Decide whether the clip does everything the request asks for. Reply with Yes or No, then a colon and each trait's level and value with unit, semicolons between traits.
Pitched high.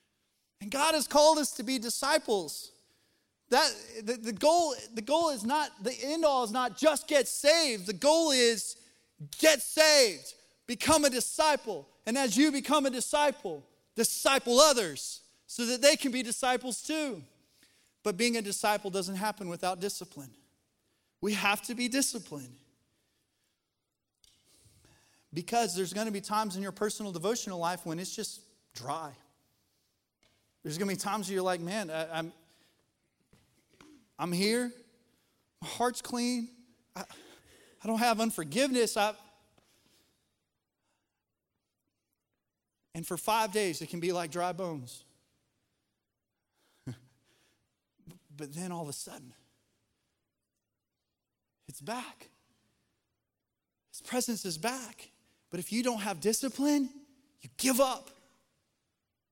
Yes: high, 220 Hz